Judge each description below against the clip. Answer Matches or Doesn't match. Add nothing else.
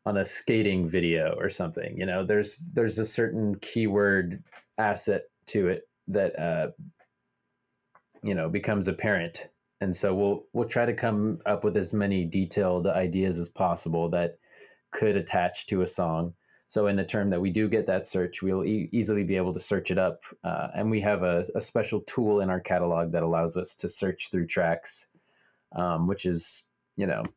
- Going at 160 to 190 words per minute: Matches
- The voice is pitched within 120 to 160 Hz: Doesn't match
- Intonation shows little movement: Doesn't match